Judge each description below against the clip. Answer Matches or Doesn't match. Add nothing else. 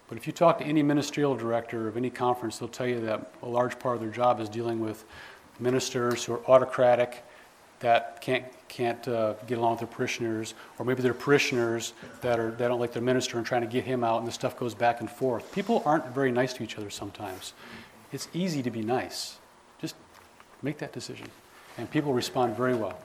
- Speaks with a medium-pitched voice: Doesn't match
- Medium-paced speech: Doesn't match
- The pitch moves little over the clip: Matches